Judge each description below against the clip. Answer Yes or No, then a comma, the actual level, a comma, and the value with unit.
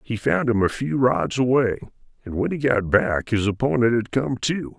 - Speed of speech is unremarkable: No, fast, 215 wpm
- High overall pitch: No, low, 120 Hz